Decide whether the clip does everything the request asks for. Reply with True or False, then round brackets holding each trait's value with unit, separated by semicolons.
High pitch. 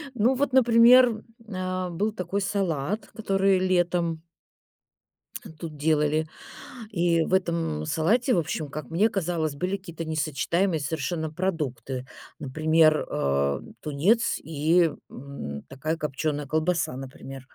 False (165 Hz)